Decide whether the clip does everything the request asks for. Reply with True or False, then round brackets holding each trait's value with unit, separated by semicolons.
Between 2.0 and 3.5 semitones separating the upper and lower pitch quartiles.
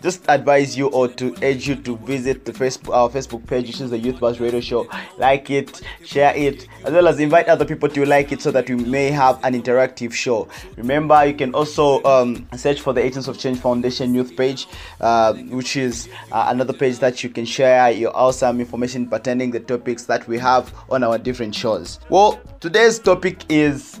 True (2.4 semitones)